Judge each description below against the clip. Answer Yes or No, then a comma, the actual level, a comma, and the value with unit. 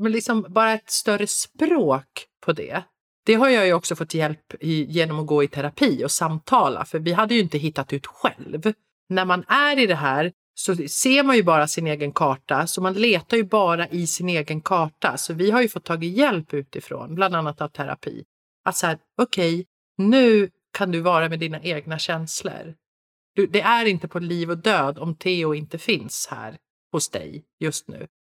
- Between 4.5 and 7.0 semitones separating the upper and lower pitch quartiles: Yes, average, 5.0 semitones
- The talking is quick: Yes, fast, 200 wpm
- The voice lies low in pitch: No, medium, 175 Hz